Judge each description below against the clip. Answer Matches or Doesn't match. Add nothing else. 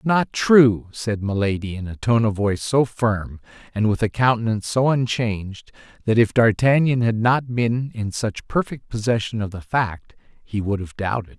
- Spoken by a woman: Doesn't match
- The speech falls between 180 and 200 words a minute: Matches